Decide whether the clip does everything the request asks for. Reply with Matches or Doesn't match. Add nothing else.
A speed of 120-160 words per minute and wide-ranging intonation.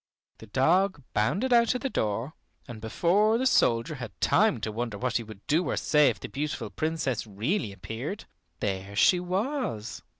Doesn't match